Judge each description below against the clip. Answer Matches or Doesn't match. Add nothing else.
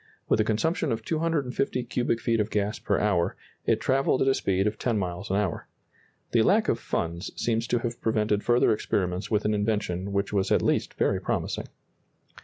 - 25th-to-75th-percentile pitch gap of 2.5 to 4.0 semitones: Matches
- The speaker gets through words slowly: Doesn't match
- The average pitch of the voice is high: Doesn't match